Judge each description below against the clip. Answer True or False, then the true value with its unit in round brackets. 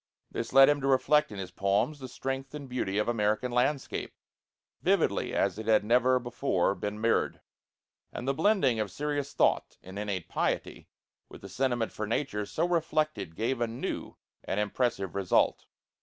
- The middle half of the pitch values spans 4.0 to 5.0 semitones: True (4.6 semitones)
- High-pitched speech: False (120 Hz)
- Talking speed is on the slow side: False (170 wpm)